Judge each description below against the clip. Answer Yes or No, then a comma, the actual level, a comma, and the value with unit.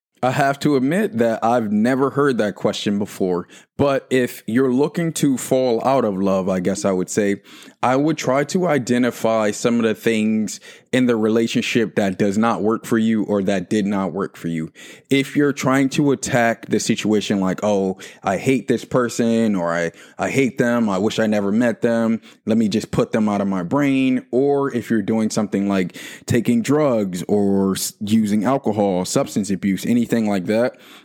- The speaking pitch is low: Yes, low, 115 Hz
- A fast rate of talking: No, average, 190 wpm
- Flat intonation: No, average, 4.3 semitones